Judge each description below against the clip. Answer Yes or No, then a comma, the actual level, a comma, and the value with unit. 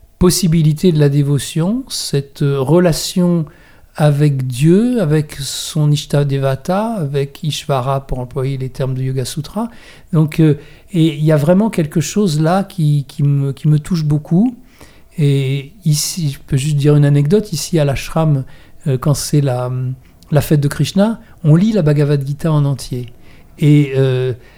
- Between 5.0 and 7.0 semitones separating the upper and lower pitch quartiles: No, average, 3.1 semitones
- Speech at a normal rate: Yes, average, 155 wpm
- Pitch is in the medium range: Yes, medium, 150 Hz